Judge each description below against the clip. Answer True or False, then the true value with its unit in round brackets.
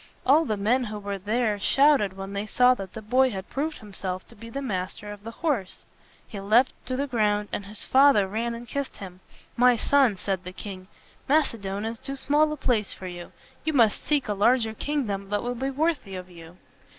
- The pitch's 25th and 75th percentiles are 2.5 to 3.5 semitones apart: False (4.8 semitones)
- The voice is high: True (220 Hz)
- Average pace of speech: False (210 wpm)